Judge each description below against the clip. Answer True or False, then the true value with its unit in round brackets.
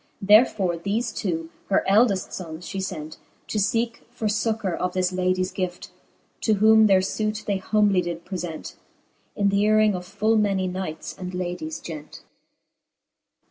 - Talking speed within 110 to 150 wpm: True (145 wpm)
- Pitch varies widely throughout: False (2.9 semitones)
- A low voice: False (190 Hz)